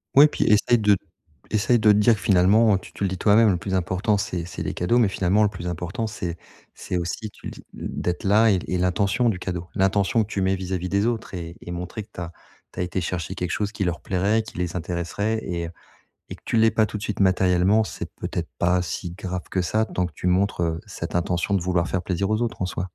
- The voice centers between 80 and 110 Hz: Yes, very low, 95 Hz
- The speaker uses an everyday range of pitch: Yes, average, 3.0 semitones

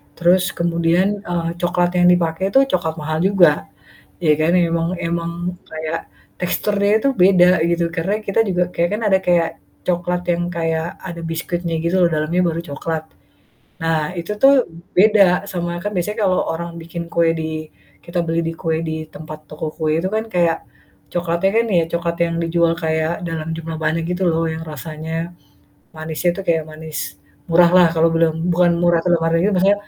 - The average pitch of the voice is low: No, medium, 170 Hz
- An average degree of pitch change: No, narrow, 1.5 semitones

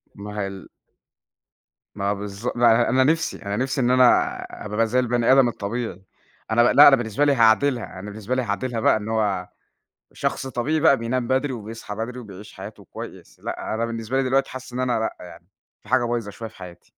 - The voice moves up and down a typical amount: Yes, average, 3.6 semitones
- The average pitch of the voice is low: Yes, low, 115 Hz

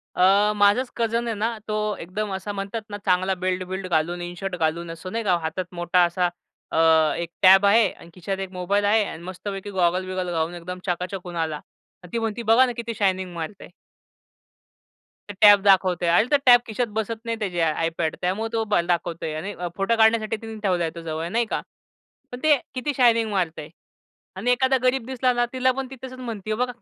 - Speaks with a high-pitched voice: Yes, high, 195 Hz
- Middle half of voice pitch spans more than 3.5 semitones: Yes, average, 4.2 semitones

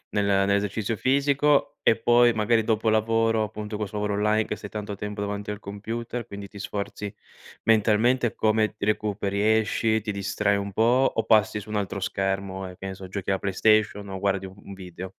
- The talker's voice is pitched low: Yes, low, 105 Hz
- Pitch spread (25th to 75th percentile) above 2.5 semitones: No, narrow, 1.8 semitones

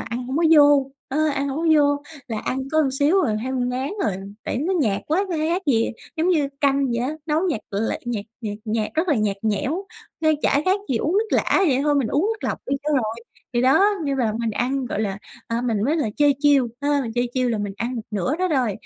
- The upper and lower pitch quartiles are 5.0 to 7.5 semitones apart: No, average, 4.6 semitones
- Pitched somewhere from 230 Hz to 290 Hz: Yes, very high, 270 Hz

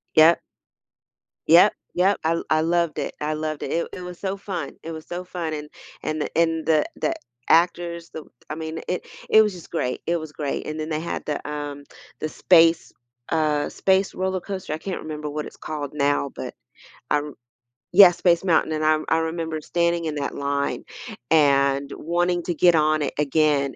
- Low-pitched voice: No, medium, 160 Hz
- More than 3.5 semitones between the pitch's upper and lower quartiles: No, narrow, 2.4 semitones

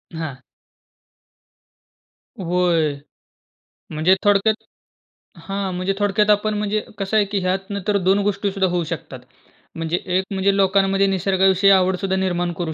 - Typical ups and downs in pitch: No, narrow, 1.8 semitones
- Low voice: No, high, 190 Hz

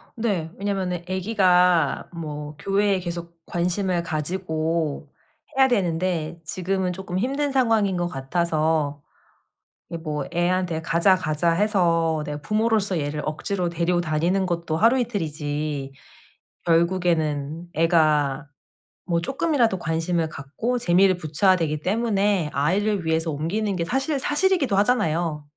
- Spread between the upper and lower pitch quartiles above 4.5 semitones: No, average, 3.8 semitones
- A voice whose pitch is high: No, medium, 175 Hz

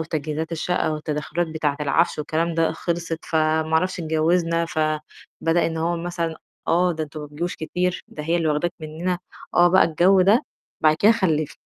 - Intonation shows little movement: Yes, narrow, 1.9 semitones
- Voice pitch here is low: No, medium, 165 Hz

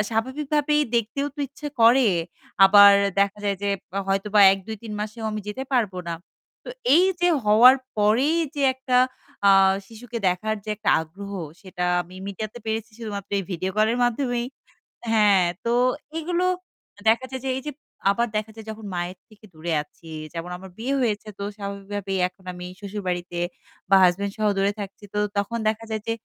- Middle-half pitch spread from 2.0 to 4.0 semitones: Yes, average, 3.4 semitones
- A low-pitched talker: No, high, 215 Hz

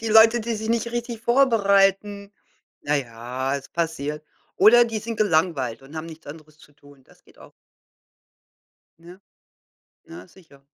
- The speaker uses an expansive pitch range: Yes, wide, 7.5 semitones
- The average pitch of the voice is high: No, medium, 175 Hz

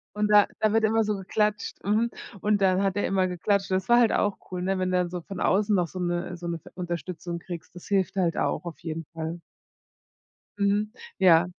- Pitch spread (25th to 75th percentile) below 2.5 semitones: No, average, 2.9 semitones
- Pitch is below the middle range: No, medium, 185 Hz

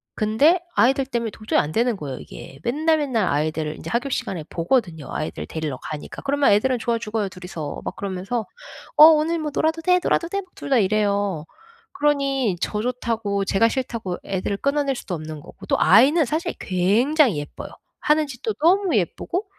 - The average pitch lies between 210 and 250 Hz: Yes, high, 230 Hz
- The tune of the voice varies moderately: No, wide, 7.4 semitones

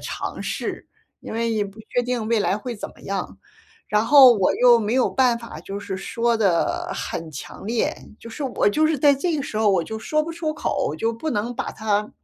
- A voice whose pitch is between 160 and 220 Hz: No, high, 230 Hz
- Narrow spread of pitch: No, average, 3.9 semitones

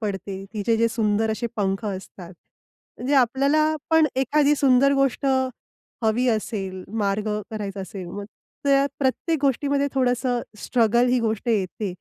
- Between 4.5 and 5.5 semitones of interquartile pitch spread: Yes, average, 4.9 semitones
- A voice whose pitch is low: No, high, 230 Hz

